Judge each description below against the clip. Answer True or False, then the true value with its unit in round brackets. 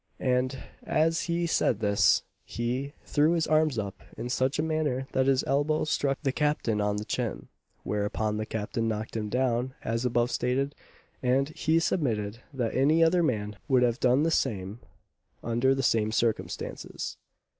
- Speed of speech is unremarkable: True (165 wpm)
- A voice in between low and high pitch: False (130 Hz)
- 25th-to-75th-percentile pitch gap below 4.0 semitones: False (4.6 semitones)